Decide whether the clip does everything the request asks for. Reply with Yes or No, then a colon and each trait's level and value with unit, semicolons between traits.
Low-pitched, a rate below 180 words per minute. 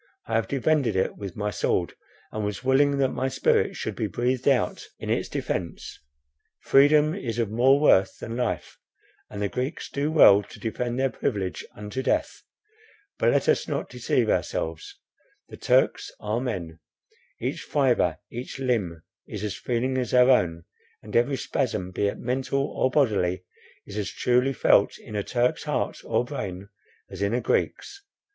Yes: low, 120 Hz; average, 170 wpm